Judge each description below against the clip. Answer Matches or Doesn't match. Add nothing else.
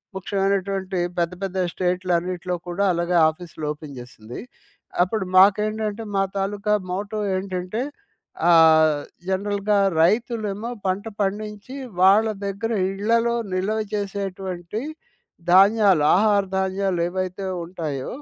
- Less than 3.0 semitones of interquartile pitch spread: Matches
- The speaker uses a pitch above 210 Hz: Doesn't match